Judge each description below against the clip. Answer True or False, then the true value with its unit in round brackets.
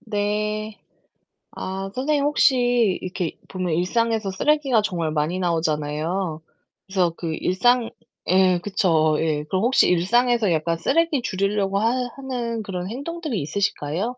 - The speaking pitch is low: False (195 Hz)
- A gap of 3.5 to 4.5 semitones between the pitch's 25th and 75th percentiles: False (5.5 semitones)